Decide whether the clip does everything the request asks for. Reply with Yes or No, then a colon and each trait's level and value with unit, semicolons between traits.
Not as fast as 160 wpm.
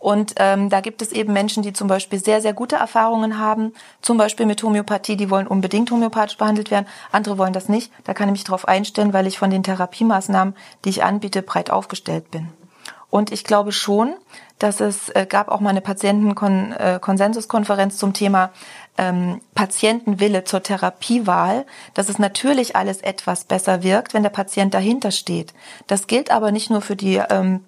No: average, 180 wpm